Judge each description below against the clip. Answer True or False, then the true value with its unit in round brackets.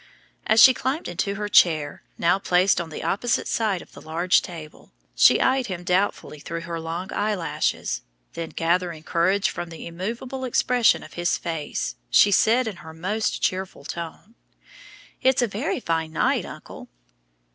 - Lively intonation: False (4.5 semitones)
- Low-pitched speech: False (180 Hz)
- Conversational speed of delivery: True (160 wpm)